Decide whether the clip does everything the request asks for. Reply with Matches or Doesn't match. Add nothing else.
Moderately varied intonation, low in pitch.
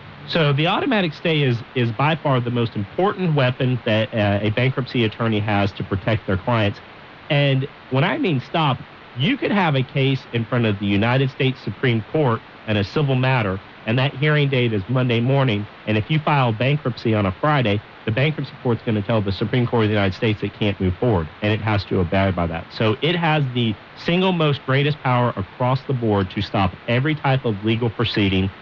Matches